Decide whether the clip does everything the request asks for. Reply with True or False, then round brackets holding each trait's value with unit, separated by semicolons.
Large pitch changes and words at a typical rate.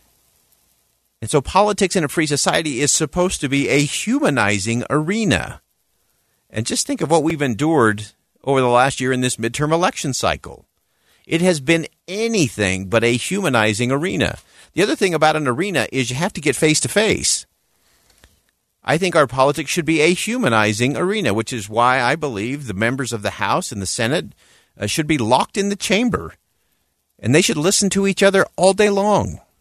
True (7.1 semitones; 180 wpm)